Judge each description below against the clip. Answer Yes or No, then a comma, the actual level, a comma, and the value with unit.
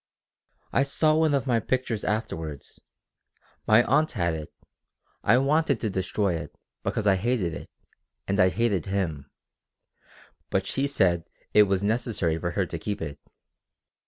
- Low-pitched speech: Yes, low, 100 Hz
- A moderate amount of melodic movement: No, wide, 6.0 semitones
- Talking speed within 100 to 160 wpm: Yes, average, 150 wpm